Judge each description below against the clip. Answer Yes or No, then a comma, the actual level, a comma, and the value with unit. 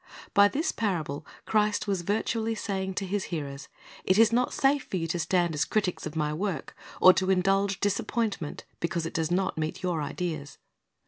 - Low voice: No, medium, 185 Hz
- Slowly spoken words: No, average, 185 wpm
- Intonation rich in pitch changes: No, average, 4.0 semitones